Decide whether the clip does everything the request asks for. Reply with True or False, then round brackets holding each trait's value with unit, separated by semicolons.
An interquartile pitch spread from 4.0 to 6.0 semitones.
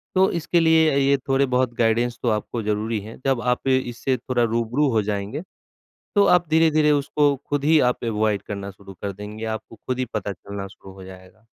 True (5.0 semitones)